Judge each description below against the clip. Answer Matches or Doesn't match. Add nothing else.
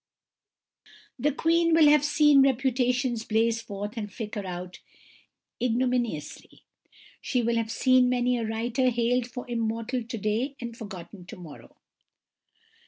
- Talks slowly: Matches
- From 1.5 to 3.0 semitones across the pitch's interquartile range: Matches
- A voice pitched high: Matches